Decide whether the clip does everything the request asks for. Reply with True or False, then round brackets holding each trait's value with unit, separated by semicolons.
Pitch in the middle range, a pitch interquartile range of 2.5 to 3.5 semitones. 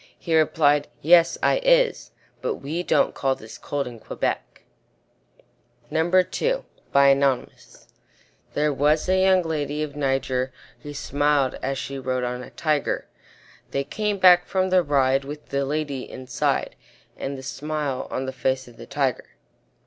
True (145 Hz; 3.2 semitones)